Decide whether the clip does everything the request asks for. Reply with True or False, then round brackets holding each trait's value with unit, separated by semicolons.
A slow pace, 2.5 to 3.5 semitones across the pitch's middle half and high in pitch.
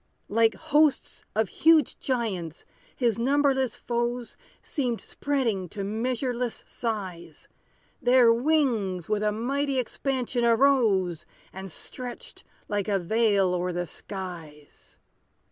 False (110 wpm; 5.0 semitones; 230 Hz)